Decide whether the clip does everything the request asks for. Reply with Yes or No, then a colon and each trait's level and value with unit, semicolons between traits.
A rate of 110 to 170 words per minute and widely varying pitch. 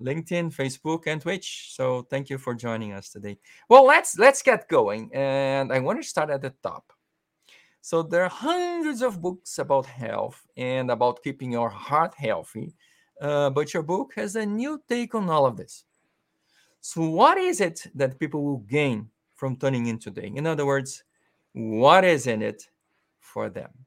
No: average, 180 wpm; wide, 5.7 semitones